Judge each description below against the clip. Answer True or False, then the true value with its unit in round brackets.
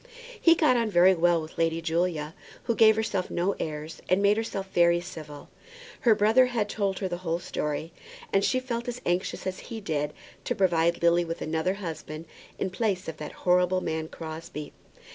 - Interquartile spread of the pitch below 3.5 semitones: False (4.0 semitones)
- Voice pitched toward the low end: False (180 Hz)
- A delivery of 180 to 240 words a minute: True (185 wpm)